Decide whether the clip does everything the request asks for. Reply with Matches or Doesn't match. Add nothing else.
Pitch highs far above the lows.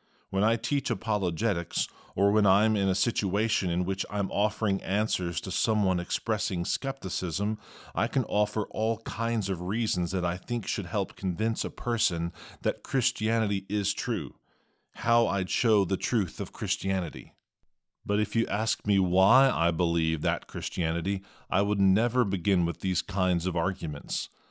Doesn't match